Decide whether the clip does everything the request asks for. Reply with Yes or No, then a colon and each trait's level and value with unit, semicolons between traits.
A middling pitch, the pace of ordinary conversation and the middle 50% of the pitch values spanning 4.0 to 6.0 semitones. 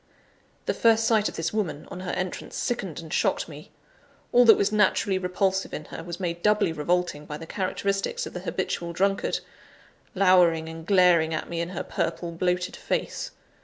No: medium, 180 Hz; average, 180 wpm; average, 2.9 semitones